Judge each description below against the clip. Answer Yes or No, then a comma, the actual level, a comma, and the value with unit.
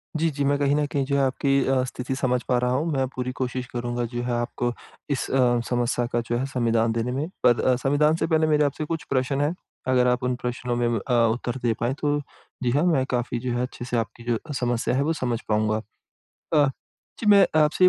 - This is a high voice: No, low, 125 Hz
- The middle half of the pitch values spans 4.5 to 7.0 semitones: No, average, 2.8 semitones